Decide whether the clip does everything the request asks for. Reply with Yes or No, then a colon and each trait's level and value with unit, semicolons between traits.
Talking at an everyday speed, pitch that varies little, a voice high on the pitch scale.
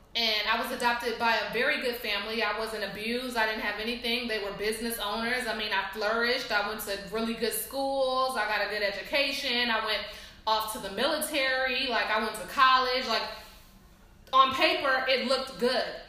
No: average, 195 wpm; average, 3.2 semitones; high, 225 Hz